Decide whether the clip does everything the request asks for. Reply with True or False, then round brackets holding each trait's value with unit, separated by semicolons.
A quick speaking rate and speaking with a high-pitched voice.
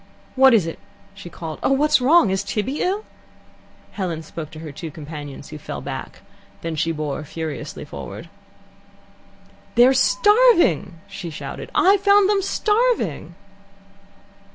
False (135 wpm; 195 Hz)